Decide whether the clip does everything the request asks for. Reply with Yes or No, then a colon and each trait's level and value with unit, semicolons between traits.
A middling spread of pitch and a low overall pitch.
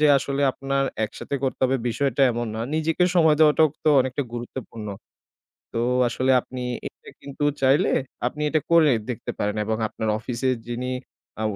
Yes: average, 3.7 semitones; low, 130 Hz